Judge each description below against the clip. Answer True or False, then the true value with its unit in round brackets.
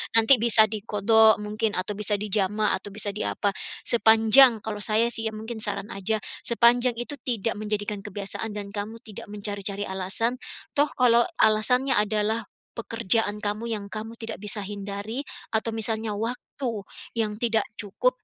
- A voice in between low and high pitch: False (215 Hz)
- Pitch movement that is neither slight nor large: False (1.8 semitones)